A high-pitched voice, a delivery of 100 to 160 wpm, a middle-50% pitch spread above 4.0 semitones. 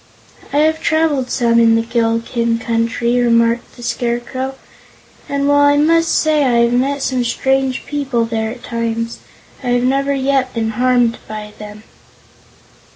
No: high, 245 Hz; average, 155 wpm; average, 2.9 semitones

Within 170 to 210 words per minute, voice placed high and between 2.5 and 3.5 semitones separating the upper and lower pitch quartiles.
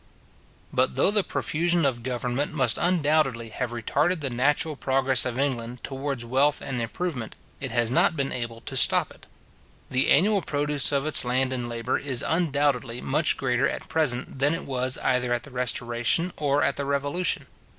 No: average, 175 wpm; low, 135 Hz; average, 3.2 semitones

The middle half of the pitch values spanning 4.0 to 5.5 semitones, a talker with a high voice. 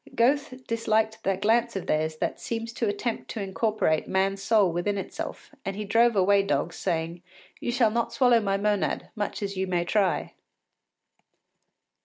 No: average, 3.2 semitones; high, 205 Hz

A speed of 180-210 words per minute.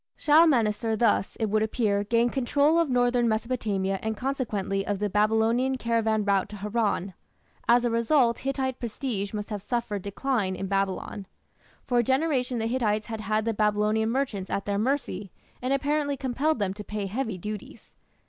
No: average, 165 wpm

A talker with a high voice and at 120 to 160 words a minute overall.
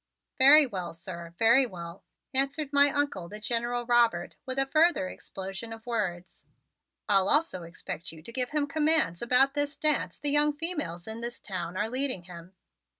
No: high, 235 Hz; average, 170 wpm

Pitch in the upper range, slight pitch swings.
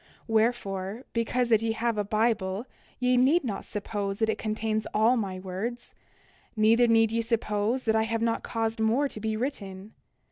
Yes: high, 225 Hz; narrow, 1.9 semitones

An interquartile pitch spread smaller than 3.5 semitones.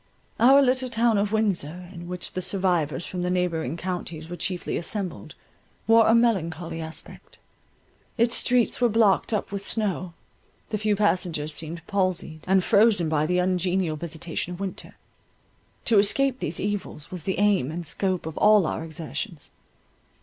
No: average, 4.0 semitones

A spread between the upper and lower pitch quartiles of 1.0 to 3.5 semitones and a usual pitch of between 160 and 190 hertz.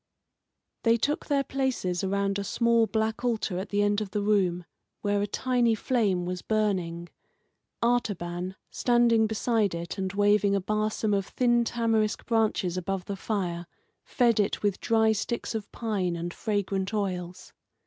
No: average, 3.2 semitones; high, 205 Hz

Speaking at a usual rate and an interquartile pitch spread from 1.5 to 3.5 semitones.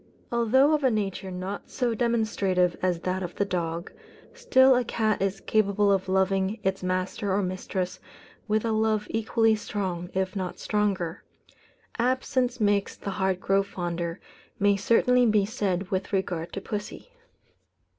Yes: average, 150 wpm; average, 3.0 semitones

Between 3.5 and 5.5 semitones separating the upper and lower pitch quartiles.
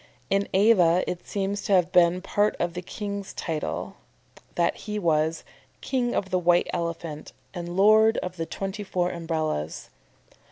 No: average, 3.0 semitones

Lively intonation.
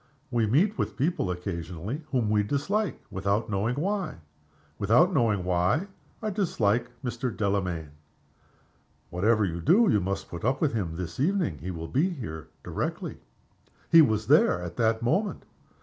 Yes: wide, 7.8 semitones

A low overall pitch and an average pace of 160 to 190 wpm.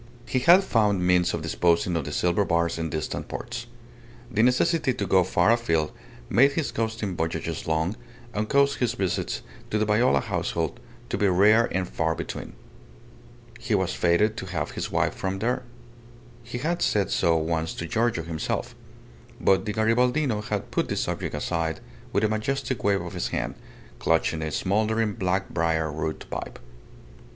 Yes: low, 100 Hz; average, 170 wpm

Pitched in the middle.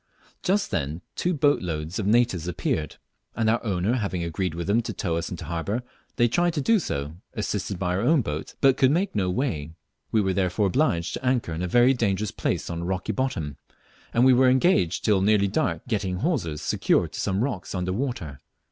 No: low, 100 Hz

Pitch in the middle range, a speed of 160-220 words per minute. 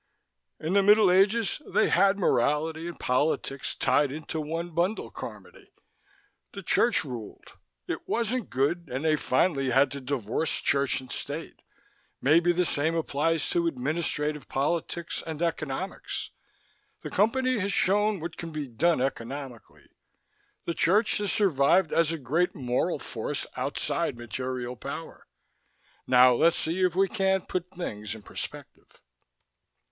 No: medium, 160 Hz; average, 140 wpm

